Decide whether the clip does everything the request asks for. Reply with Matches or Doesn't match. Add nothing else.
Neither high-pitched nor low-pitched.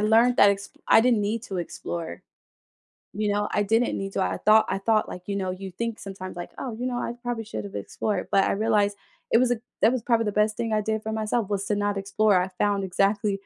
Doesn't match